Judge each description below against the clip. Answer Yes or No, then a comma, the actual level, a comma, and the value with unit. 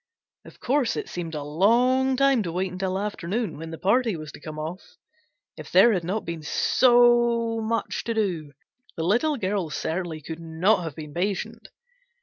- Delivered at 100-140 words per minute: No, average, 175 wpm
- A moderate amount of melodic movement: No, wide, 6.2 semitones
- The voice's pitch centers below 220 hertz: Yes, high, 190 Hz